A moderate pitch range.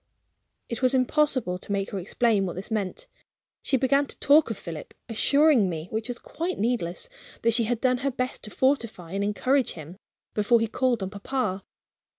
Yes: average, 4.8 semitones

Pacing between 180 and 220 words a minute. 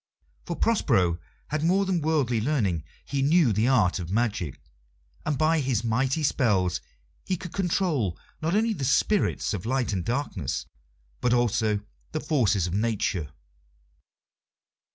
No: average, 140 wpm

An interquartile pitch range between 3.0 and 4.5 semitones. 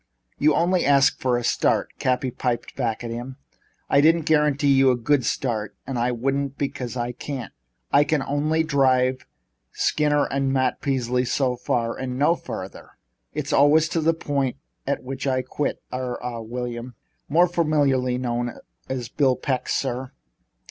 No: narrow, 2.6 semitones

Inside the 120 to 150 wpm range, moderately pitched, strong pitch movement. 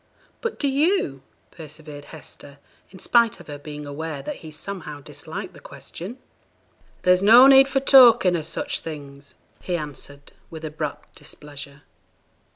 Yes: average, 145 wpm; medium, 160 Hz; wide, 7.5 semitones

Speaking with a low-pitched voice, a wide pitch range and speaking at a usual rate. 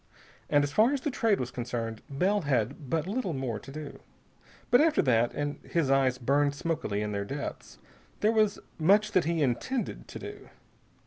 No: medium, 145 Hz; wide, 8.0 semitones; average, 185 wpm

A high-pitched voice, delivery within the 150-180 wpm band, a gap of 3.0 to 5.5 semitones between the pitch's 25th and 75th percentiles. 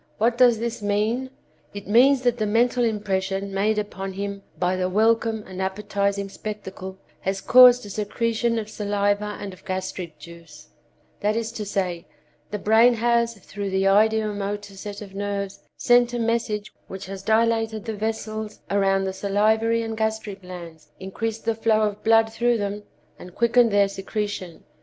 No: high, 210 Hz; average, 165 wpm; narrow, 2.5 semitones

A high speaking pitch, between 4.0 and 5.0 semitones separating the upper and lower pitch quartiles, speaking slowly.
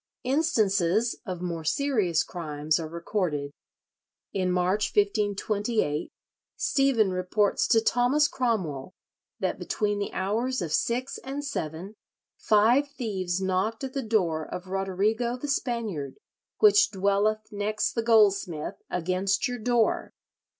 Yes: high, 205 Hz; average, 4.6 semitones; slow, 120 wpm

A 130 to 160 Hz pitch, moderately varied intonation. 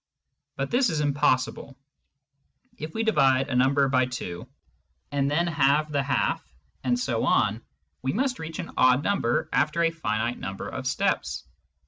Yes: medium, 140 Hz; average, 4.0 semitones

